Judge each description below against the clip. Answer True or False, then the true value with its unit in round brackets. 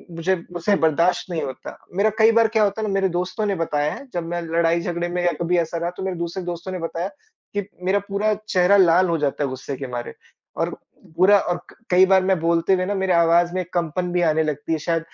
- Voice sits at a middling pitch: True (175 Hz)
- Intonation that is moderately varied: False (2.3 semitones)